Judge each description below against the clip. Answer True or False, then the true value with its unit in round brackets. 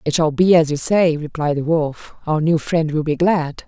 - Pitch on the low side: False (160 Hz)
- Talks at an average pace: False (245 wpm)